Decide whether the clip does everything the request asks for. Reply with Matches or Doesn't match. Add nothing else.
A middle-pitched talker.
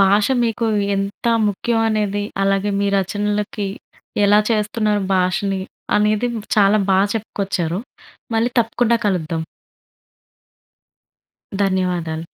Doesn't match